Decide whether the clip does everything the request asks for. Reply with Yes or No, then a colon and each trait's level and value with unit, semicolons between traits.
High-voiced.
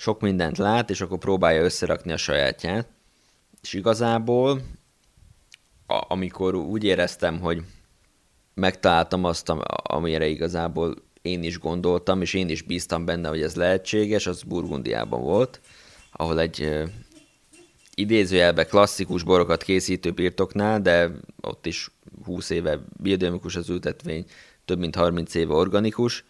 No: very low, 90 Hz